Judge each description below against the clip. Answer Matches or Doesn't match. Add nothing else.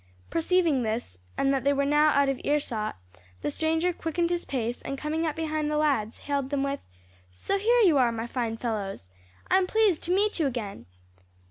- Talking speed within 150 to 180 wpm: Doesn't match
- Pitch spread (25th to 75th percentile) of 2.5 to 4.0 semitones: Doesn't match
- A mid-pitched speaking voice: Doesn't match